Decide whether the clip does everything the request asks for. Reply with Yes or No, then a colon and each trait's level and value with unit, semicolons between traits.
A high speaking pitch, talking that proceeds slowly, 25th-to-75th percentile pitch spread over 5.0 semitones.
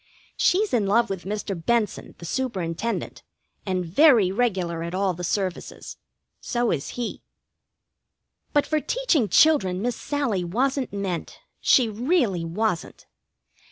Yes: high, 210 Hz; slow, 125 wpm; wide, 5.5 semitones